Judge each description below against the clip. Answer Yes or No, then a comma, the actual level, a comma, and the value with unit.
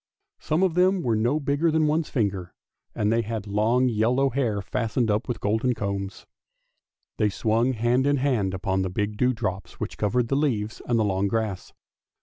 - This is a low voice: Yes, low, 115 Hz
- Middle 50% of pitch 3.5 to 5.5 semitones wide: Yes, average, 4.2 semitones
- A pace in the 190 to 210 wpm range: No, average, 180 wpm